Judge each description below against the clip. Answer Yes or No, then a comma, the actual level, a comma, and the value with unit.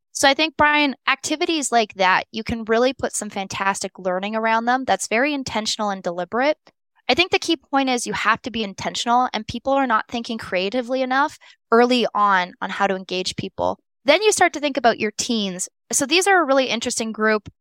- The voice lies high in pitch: Yes, high, 235 Hz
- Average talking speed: No, fast, 210 wpm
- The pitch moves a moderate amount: Yes, average, 4.9 semitones